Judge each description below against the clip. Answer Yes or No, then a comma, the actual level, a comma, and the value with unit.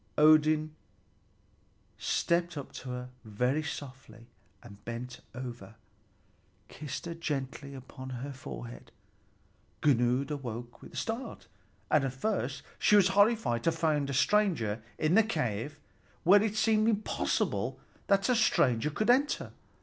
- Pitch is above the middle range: No, medium, 145 Hz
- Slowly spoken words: Yes, slow, 130 wpm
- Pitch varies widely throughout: Yes, wide, 7.8 semitones